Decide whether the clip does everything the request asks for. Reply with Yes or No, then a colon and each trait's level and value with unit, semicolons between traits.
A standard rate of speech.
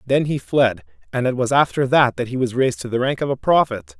No: fast, 270 wpm